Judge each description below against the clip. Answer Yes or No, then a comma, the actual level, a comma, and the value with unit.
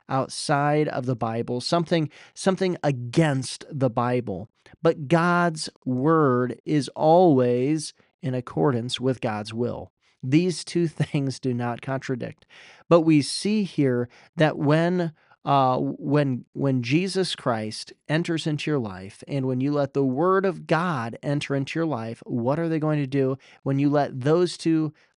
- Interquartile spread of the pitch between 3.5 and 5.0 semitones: Yes, average, 4.1 semitones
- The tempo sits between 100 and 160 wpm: Yes, average, 150 wpm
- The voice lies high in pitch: No, medium, 145 Hz